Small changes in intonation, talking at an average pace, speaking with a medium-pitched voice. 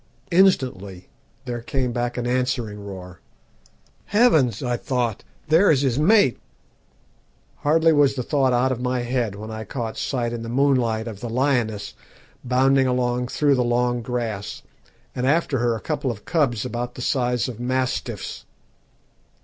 No: narrow, 2.3 semitones; average, 155 wpm; low, 125 Hz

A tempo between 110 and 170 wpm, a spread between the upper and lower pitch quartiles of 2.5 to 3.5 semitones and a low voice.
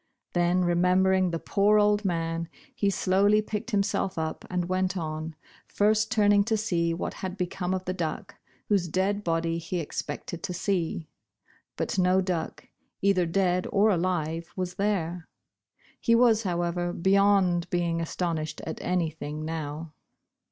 No: average, 145 wpm; average, 3.0 semitones; medium, 180 Hz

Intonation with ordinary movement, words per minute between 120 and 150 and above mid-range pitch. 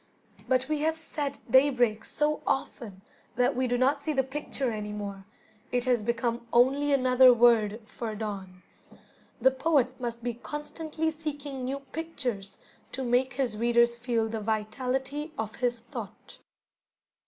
Yes: average, 3.4 semitones; average, 145 wpm; very high, 250 Hz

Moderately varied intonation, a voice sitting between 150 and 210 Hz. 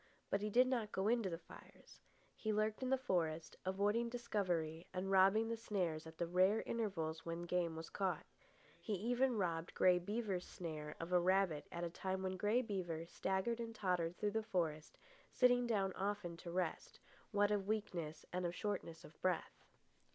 Yes: average, 3.9 semitones; high, 190 Hz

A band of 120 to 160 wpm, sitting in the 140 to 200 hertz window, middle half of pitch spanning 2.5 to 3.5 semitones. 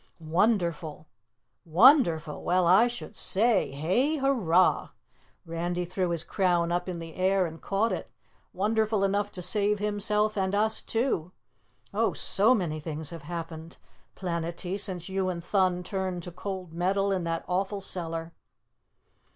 Yes: average, 145 wpm; medium, 185 Hz; average, 3.2 semitones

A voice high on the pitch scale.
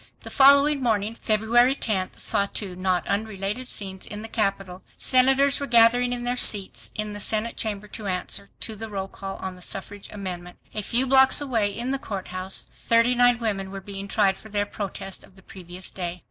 Yes: high, 210 Hz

